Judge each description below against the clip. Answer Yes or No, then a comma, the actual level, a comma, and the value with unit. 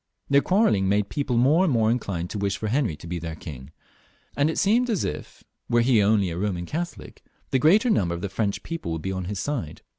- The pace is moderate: No, fast, 235 wpm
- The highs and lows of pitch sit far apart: Yes, wide, 8.1 semitones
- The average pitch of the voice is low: Yes, low, 105 Hz